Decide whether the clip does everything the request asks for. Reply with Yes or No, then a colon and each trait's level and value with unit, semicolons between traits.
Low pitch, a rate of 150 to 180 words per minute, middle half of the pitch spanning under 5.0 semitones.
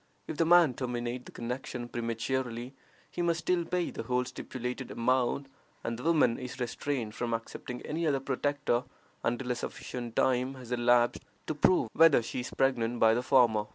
Yes: low, 125 Hz; average, 175 wpm; narrow, 2.6 semitones